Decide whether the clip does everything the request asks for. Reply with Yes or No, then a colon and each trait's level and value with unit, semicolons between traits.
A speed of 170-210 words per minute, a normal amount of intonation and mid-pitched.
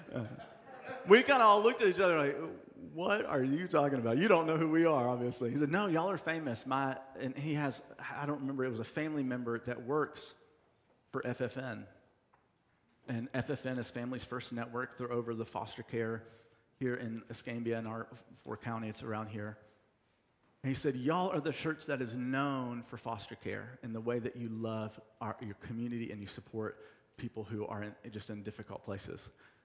No: average, 190 wpm; average, 3.5 semitones; low, 125 Hz